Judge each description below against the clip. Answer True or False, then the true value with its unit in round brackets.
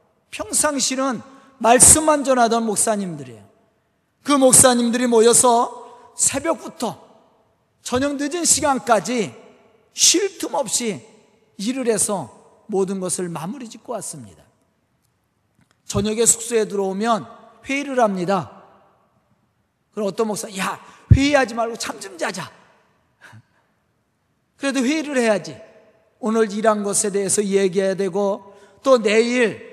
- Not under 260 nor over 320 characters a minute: False (240 characters per minute)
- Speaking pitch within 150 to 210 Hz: False (225 Hz)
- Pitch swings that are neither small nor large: True (4.2 semitones)